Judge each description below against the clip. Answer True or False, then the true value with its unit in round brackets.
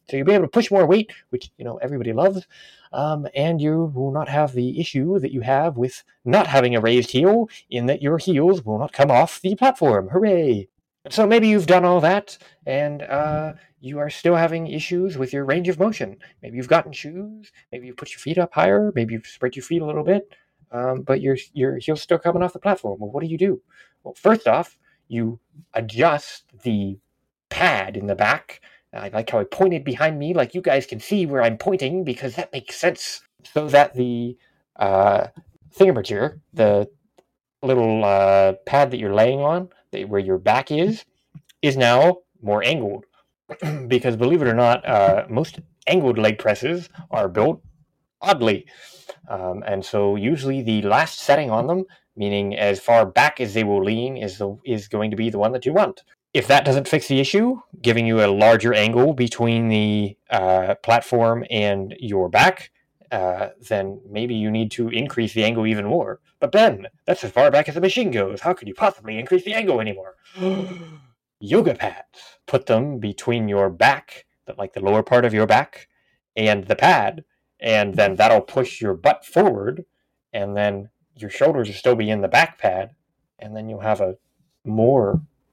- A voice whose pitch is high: False (135 Hz)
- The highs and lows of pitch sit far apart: True (7.1 semitones)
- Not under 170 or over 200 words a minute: True (190 wpm)